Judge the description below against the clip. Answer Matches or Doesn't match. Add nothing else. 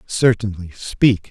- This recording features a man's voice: Matches